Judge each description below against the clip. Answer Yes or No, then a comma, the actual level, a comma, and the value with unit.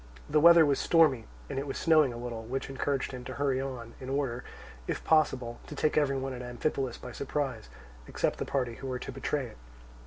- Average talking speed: No, fast, 215 wpm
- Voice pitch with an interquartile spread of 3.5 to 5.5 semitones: No, narrow, 2.5 semitones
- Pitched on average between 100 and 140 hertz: Yes, low, 135 Hz